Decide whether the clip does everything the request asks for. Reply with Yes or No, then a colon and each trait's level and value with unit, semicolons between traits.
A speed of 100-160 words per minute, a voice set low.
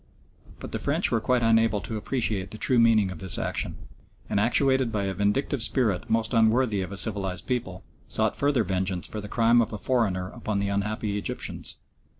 No: average, 190 wpm; low, 110 Hz